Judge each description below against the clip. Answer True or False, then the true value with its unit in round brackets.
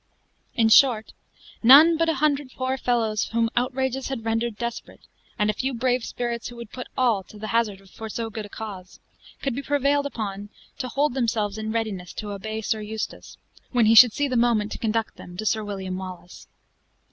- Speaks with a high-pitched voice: True (230 Hz)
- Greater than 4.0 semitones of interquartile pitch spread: False (3.1 semitones)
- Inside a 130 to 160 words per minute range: False (200 wpm)